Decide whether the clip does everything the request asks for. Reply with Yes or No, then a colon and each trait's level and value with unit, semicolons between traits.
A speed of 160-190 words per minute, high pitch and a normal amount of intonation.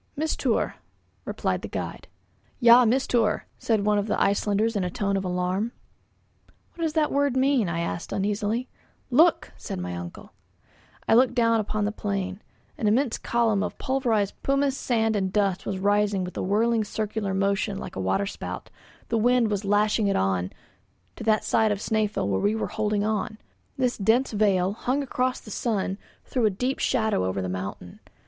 Yes: average, 175 wpm; high, 210 Hz; average, 3.2 semitones